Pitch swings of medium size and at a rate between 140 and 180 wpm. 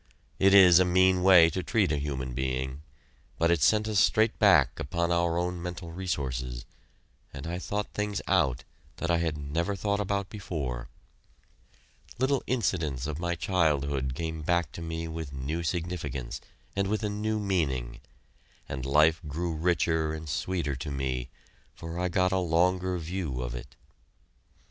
Yes: average, 4.6 semitones; average, 160 wpm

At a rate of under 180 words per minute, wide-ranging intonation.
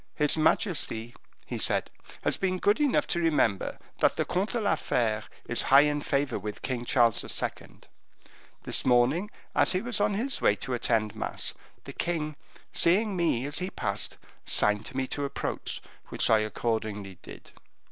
Yes: average, 170 wpm; wide, 8.2 semitones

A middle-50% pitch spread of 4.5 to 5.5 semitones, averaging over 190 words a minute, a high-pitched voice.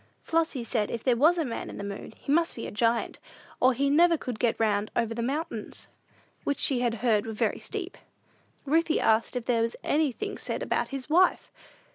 Yes: average, 5.0 semitones; fast, 205 wpm; very high, 250 Hz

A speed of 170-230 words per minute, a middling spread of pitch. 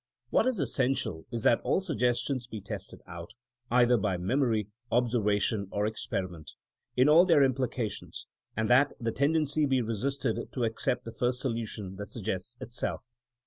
No: average, 155 wpm; average, 4.1 semitones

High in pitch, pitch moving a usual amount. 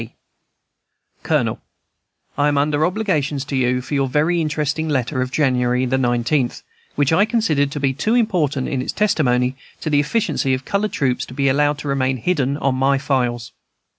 No: medium, 140 Hz; average, 3.0 semitones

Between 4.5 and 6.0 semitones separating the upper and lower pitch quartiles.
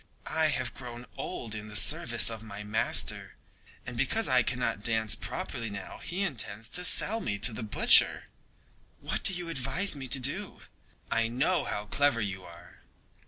Yes: wide, 5.5 semitones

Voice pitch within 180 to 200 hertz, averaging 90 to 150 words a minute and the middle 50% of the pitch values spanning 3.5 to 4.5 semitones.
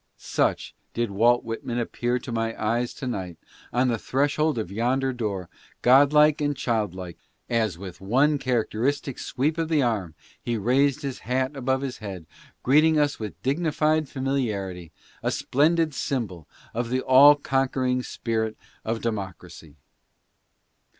No: low, 125 Hz; average, 140 wpm; average, 4.1 semitones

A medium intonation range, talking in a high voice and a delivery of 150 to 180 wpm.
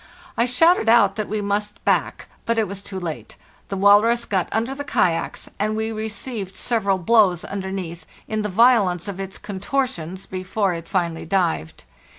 Yes: average, 3.2 semitones; high, 200 Hz; average, 165 wpm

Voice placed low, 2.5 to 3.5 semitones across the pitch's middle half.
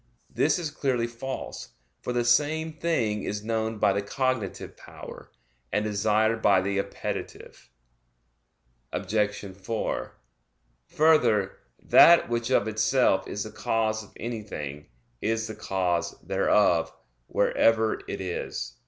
Yes: low, 110 Hz; average, 2.9 semitones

